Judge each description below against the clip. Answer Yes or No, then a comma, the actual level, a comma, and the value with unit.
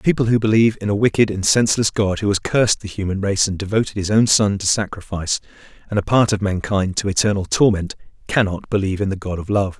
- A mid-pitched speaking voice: No, low, 100 Hz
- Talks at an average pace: No, fast, 215 wpm